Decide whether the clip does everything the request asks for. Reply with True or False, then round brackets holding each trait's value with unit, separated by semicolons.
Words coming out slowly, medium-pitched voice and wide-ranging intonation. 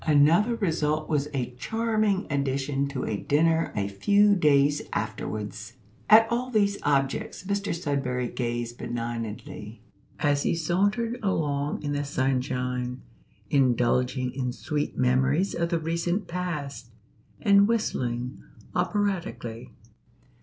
True (115 wpm; 145 Hz; 6.2 semitones)